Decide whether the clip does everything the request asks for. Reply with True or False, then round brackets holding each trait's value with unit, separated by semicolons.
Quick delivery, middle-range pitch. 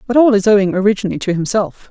False (220 wpm; 205 Hz)